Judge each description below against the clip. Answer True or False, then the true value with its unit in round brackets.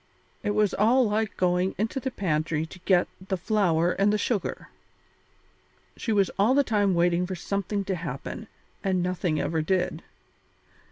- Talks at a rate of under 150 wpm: False (160 wpm)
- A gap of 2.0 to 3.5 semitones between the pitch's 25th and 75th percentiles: True (3.0 semitones)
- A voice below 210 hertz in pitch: True (190 Hz)